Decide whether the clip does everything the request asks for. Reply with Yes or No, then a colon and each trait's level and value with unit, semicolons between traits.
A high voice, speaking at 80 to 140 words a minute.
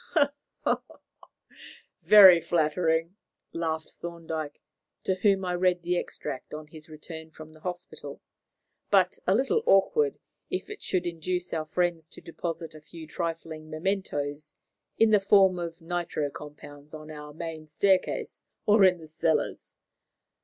No: medium, 165 Hz; slow, 135 wpm